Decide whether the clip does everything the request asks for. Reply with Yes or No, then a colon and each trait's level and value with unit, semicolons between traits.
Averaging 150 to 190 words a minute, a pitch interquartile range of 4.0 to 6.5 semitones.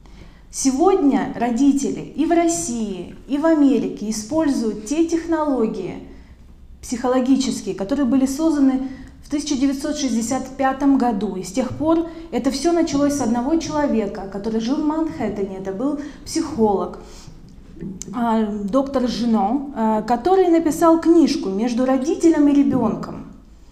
No: slow, 110 wpm; average, 5.1 semitones